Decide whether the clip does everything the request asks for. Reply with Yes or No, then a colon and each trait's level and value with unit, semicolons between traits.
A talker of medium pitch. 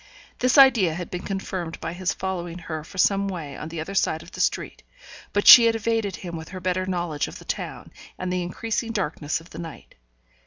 Yes: medium, 180 Hz